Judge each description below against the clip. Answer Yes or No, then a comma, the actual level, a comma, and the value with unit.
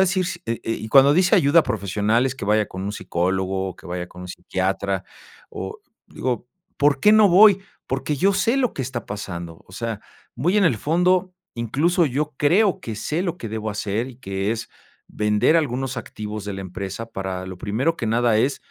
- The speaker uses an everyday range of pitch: No, wide, 7.3 semitones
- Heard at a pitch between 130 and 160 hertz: No, low, 115 Hz